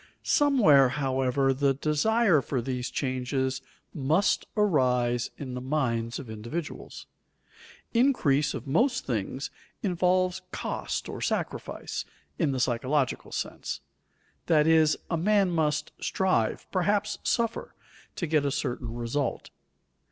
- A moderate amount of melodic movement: No, wide, 5.7 semitones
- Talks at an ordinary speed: No, slow, 115 wpm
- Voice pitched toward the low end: No, medium, 145 Hz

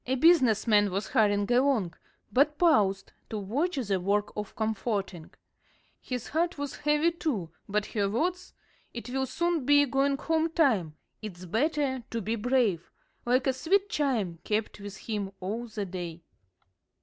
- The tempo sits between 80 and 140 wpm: No, average, 155 wpm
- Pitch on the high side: Yes, high, 230 Hz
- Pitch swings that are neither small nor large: No, wide, 6.1 semitones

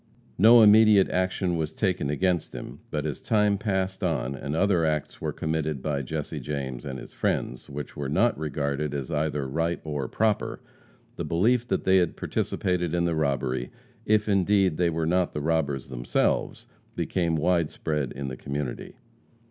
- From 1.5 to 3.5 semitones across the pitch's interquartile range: No, average, 4.6 semitones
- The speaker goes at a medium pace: Yes, average, 170 wpm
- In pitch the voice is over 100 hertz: No, very low, 80 Hz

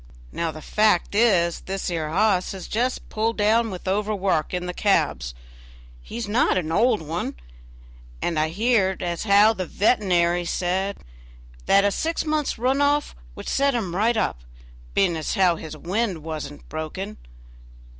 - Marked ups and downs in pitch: No, average, 4.3 semitones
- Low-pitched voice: No, high, 195 Hz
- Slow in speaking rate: No, average, 165 wpm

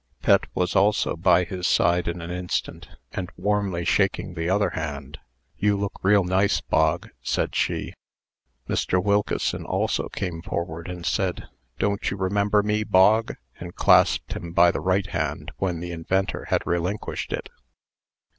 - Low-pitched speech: Yes, very low, 90 Hz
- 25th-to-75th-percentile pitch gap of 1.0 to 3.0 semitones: Yes, average, 2.7 semitones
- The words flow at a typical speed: Yes, average, 155 wpm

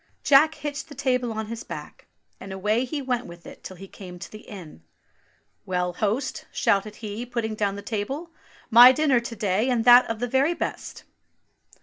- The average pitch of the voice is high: Yes, high, 230 Hz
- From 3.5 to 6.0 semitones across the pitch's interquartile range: Yes, average, 4.2 semitones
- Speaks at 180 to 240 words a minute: Yes, average, 185 wpm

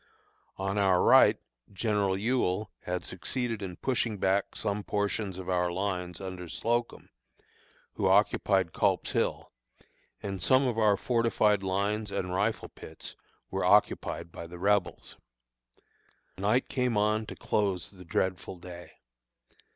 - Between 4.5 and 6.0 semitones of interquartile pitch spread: No, average, 2.7 semitones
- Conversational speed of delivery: No, slow, 130 wpm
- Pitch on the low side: Yes, low, 100 Hz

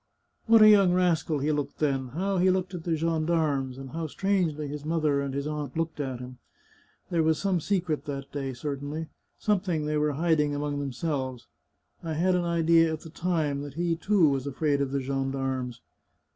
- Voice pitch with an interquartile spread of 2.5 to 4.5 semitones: Yes, average, 3.2 semitones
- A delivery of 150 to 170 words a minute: No, average, 195 wpm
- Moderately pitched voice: Yes, medium, 150 Hz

